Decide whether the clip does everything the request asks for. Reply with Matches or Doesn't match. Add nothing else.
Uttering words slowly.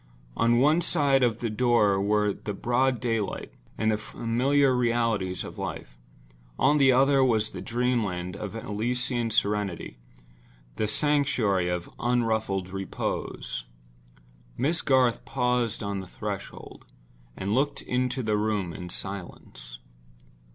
Matches